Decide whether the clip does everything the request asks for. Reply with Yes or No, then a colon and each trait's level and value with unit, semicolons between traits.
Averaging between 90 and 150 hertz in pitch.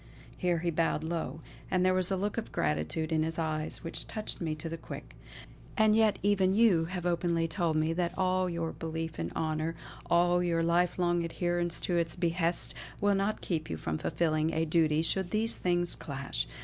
No: medium, 170 Hz